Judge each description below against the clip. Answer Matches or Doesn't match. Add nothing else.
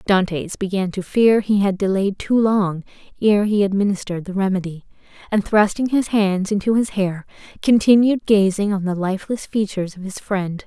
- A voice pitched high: Matches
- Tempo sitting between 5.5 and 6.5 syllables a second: Doesn't match